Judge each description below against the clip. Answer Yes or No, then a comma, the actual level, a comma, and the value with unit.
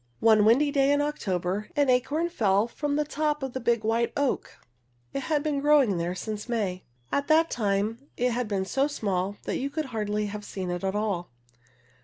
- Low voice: No, high, 235 Hz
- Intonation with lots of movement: Yes, wide, 5.8 semitones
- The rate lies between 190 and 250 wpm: Yes, average, 200 wpm